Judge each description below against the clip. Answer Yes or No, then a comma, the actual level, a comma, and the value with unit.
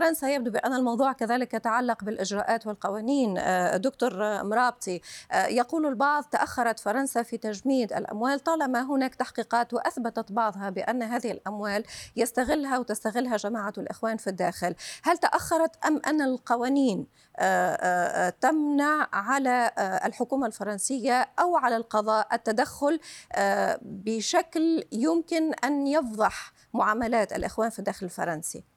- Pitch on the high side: Yes, high, 235 Hz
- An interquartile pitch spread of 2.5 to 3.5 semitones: No, average, 4.2 semitones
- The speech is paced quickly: No, average, 110 wpm